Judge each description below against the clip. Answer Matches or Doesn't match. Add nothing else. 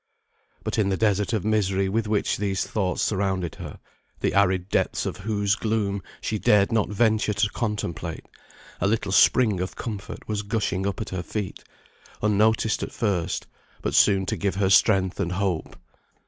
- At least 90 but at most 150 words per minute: Doesn't match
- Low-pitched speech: Matches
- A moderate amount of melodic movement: Doesn't match